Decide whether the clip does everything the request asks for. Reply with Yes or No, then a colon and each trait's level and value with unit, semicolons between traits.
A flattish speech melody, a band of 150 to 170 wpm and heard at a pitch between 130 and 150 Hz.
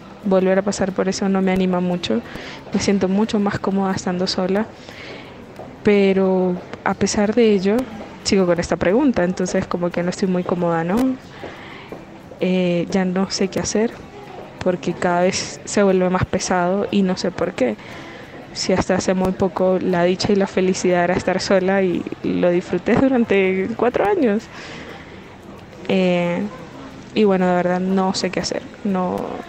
No: narrow, 2.0 semitones; average, 165 wpm; high, 190 Hz